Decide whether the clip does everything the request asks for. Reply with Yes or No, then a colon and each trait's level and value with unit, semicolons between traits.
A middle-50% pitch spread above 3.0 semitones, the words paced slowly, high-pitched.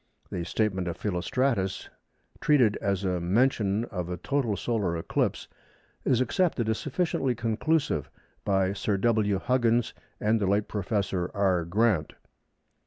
No: average, 4.1 semitones; slow, 130 wpm; low, 105 Hz